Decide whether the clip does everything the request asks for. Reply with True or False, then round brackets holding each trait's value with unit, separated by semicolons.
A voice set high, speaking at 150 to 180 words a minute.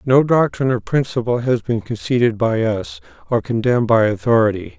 False (120 Hz; 165 wpm)